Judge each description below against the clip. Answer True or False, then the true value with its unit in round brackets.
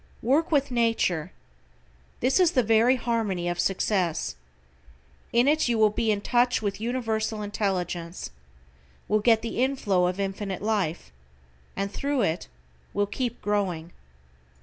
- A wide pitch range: False (4.0 semitones)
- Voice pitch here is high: True (215 Hz)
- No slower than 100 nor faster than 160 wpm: True (135 wpm)